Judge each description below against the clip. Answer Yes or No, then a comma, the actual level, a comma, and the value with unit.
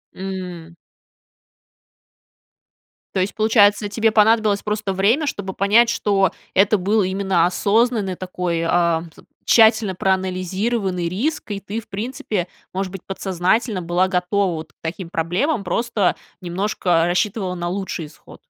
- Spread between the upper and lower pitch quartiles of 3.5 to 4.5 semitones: No, average, 2.9 semitones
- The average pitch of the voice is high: Yes, high, 195 Hz